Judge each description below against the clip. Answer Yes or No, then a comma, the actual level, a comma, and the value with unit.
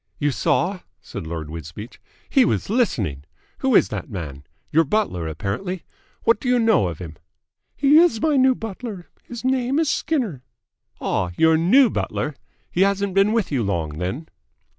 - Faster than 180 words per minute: No, average, 165 wpm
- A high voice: No, medium, 180 Hz